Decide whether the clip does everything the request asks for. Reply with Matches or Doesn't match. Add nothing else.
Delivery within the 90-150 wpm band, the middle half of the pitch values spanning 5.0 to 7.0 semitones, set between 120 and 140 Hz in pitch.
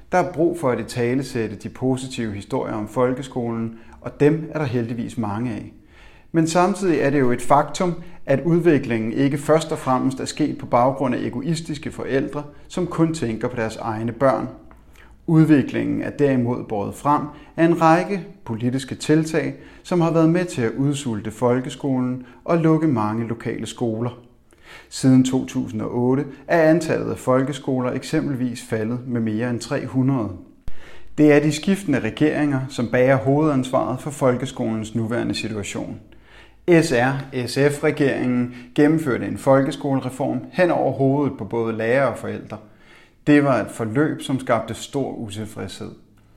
Doesn't match